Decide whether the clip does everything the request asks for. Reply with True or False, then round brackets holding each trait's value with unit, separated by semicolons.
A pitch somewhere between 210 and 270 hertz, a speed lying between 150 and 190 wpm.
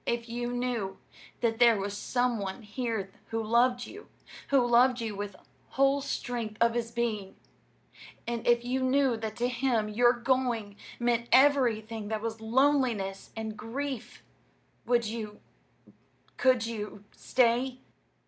False (235 Hz; 140 wpm)